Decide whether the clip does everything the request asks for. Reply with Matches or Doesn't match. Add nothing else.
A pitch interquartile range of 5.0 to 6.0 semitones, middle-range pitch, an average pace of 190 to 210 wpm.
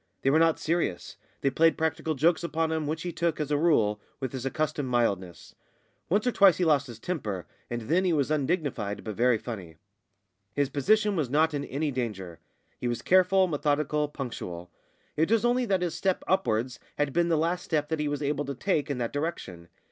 Matches